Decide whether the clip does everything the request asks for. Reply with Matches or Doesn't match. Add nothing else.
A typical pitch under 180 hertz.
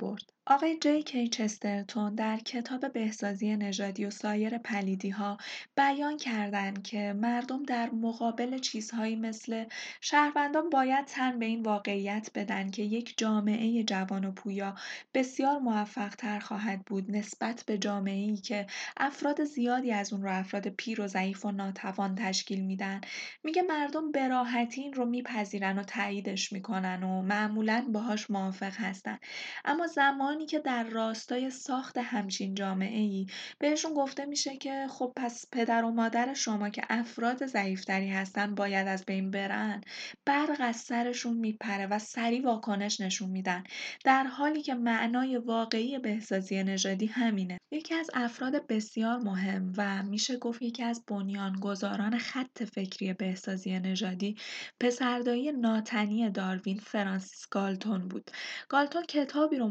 Doesn't match